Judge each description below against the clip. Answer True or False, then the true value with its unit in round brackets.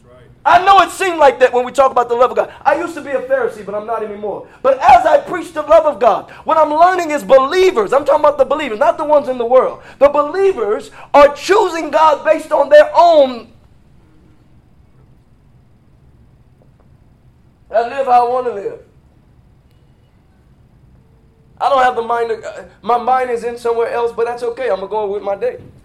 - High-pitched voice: True (280 Hz)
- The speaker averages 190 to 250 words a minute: True (200 wpm)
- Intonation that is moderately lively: True (4.8 semitones)